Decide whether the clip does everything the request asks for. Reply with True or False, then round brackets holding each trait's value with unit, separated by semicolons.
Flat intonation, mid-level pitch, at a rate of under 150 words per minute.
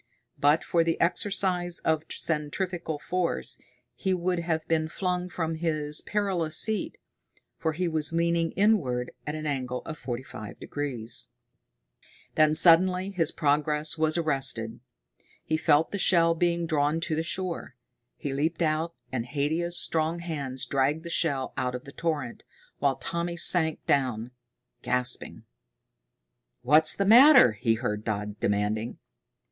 False (3.8 semitones; 155 Hz; 140 wpm)